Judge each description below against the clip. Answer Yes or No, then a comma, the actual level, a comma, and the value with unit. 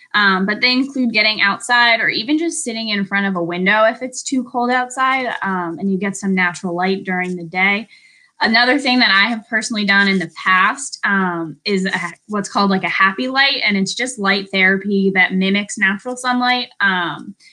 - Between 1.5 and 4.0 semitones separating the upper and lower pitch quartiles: No, average, 4.5 semitones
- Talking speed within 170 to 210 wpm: Yes, average, 200 wpm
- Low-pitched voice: No, high, 205 Hz